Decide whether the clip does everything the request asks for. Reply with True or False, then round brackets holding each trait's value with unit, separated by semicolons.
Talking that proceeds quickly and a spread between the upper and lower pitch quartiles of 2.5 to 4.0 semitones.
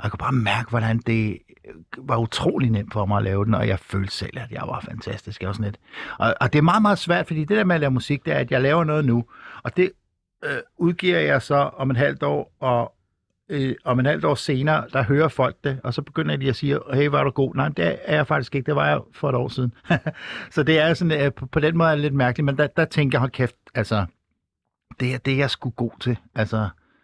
False (275 wpm; 4.9 semitones)